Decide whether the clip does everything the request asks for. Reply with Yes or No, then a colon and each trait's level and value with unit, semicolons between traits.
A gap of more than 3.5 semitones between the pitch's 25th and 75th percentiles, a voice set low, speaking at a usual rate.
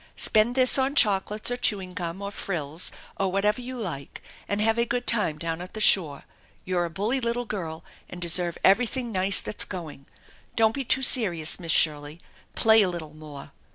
No: average, 5.2 semitones; high, 195 Hz; average, 190 wpm